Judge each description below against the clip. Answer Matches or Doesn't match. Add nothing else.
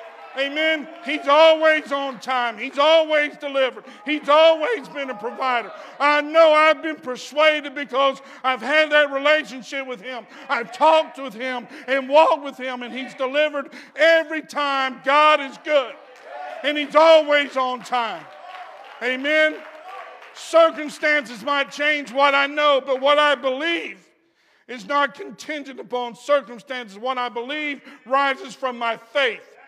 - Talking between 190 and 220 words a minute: Doesn't match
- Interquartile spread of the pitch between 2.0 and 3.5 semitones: Matches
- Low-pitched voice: Doesn't match